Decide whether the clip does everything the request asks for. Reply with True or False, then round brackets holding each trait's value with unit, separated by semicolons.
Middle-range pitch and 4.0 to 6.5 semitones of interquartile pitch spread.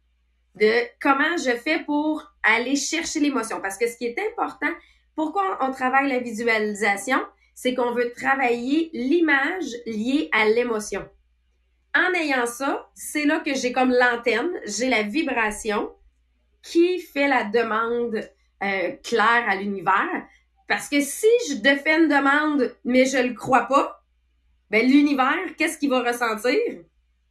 False (250 Hz; 5.2 semitones)